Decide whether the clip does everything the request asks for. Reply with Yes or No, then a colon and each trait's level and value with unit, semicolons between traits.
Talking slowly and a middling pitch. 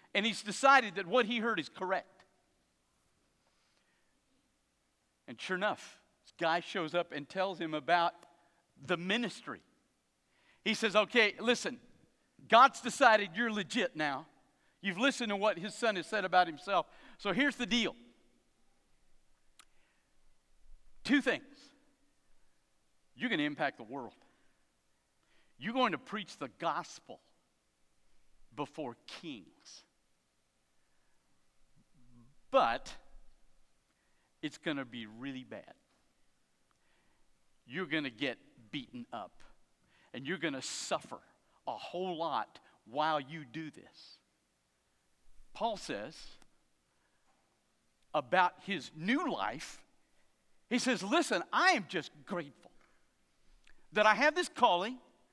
Yes: slow, 110 wpm; medium, 170 Hz